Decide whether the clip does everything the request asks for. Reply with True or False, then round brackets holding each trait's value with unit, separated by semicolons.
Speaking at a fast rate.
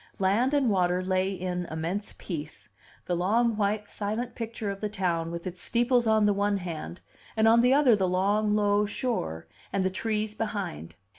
False (180 wpm)